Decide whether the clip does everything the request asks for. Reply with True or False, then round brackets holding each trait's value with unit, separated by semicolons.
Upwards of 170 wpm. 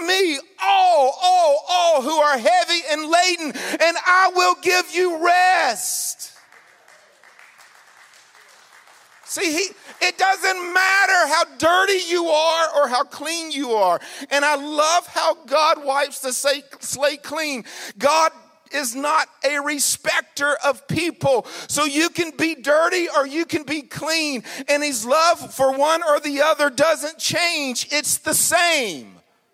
False (135 wpm)